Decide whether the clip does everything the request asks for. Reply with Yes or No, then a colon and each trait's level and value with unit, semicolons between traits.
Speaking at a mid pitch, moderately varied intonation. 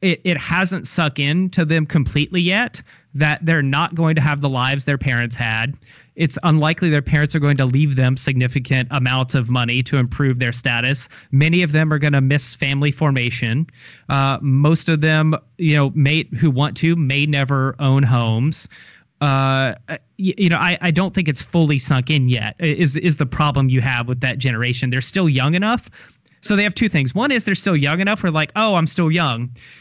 Yes: medium, 145 Hz; average, 3.6 semitones